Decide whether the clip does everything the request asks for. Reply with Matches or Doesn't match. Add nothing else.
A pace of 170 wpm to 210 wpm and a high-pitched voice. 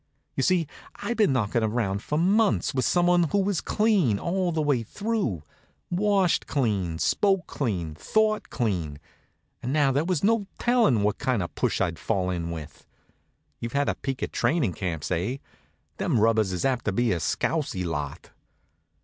Doesn't match